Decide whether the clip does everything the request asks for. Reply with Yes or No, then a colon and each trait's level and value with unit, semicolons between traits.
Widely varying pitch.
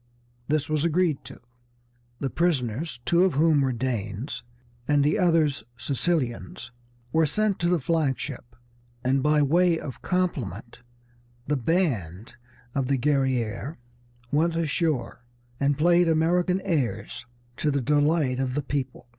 No: average, 4.4 semitones